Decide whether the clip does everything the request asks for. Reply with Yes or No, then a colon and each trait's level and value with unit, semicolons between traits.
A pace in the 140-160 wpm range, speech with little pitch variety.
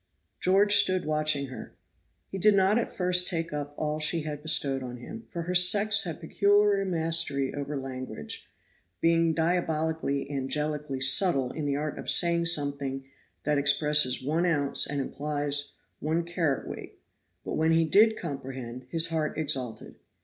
No: average, 150 wpm; average, 3.5 semitones